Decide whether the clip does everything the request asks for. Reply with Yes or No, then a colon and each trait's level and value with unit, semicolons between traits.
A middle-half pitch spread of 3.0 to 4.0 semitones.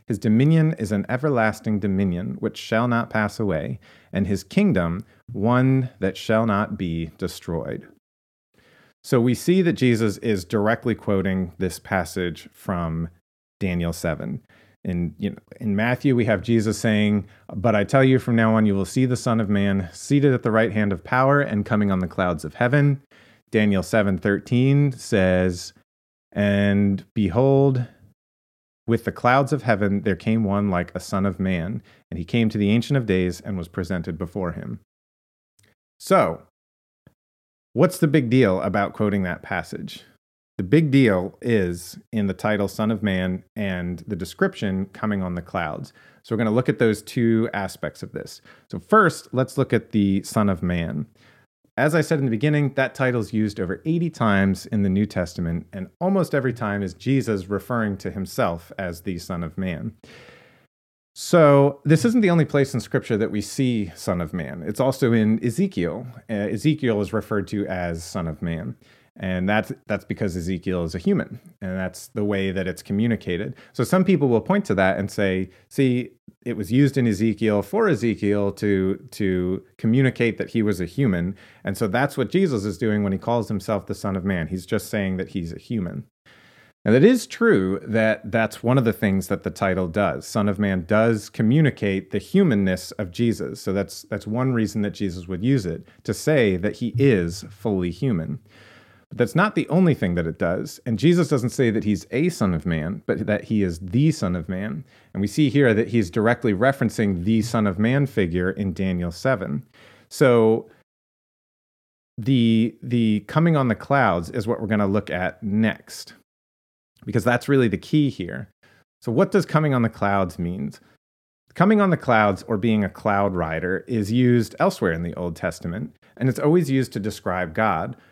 No: average, 4.6 semitones